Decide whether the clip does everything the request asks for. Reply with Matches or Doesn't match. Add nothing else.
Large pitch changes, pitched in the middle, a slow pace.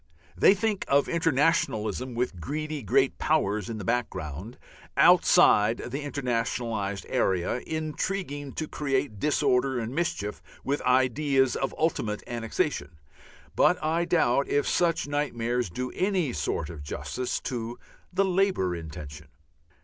Doesn't match